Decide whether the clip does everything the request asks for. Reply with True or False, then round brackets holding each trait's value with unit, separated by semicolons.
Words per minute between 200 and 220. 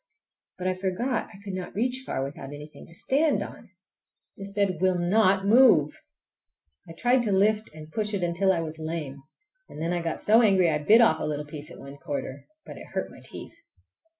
True (205 wpm)